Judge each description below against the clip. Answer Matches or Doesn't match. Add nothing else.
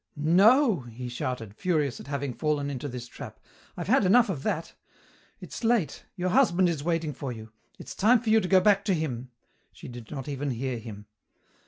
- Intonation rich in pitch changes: Matches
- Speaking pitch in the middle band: Matches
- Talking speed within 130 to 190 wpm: Doesn't match